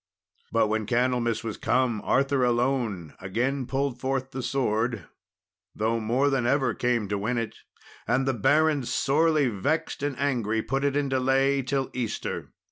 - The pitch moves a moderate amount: Yes, average, 3.1 semitones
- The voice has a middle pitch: No, low, 125 Hz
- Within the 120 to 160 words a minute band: Yes, average, 155 wpm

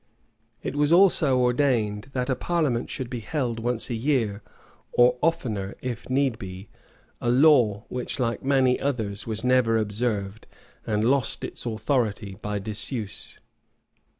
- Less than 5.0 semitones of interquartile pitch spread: Yes, average, 3.6 semitones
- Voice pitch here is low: Yes, low, 120 Hz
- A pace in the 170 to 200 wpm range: No, average, 140 wpm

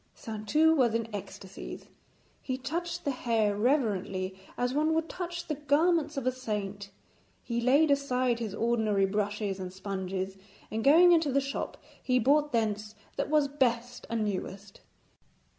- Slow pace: No, average, 150 wpm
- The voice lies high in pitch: Yes, high, 240 Hz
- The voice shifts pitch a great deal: Yes, wide, 5.7 semitones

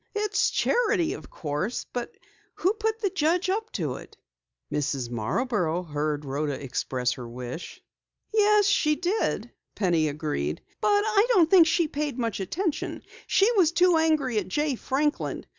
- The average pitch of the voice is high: Yes, very high, 290 Hz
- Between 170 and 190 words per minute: No, average, 150 wpm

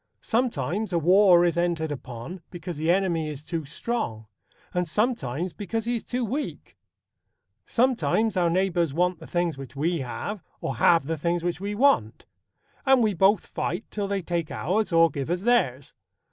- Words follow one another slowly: No, average, 175 wpm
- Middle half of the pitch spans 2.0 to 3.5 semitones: No, average, 4.5 semitones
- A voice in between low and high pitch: Yes, medium, 175 Hz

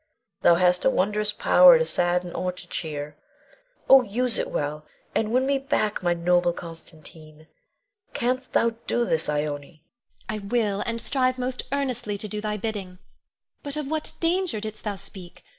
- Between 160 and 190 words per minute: Yes, average, 170 wpm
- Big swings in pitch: Yes, wide, 6.4 semitones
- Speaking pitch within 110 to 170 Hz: No, high, 210 Hz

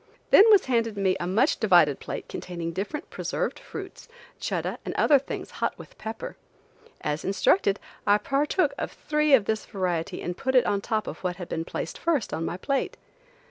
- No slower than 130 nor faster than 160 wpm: No, average, 185 wpm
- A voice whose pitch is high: Yes, high, 205 Hz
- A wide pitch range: Yes, wide, 7.1 semitones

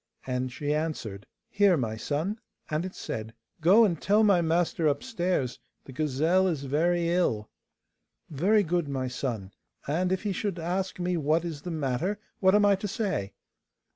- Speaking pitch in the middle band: Yes, medium, 165 Hz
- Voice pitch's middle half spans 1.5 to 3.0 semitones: No, average, 5.2 semitones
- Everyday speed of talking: Yes, average, 170 wpm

